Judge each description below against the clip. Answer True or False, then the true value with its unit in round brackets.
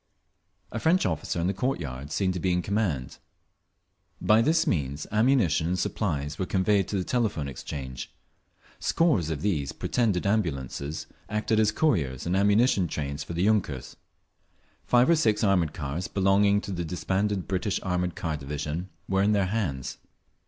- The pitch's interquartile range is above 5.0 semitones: True (5.6 semitones)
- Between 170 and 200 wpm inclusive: False (160 wpm)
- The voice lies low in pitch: True (95 Hz)